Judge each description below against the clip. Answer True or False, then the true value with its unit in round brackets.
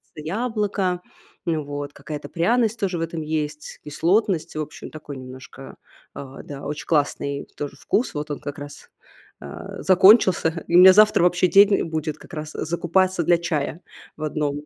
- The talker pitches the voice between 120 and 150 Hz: False (160 Hz)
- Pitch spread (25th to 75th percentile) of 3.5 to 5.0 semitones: True (4.0 semitones)